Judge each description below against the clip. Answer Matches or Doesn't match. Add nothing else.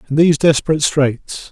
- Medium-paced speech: Matches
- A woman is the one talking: Doesn't match